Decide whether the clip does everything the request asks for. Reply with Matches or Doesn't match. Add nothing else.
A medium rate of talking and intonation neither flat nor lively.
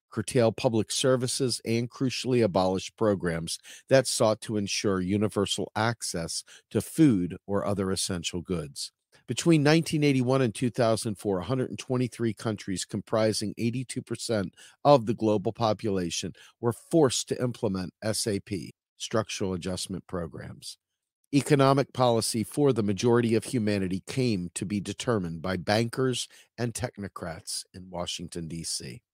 Doesn't match